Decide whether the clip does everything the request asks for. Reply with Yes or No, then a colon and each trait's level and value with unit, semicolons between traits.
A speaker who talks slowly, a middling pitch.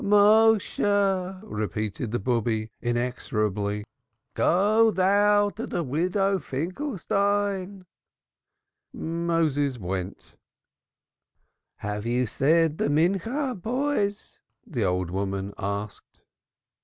Yes: slow, 85 wpm; medium, 165 Hz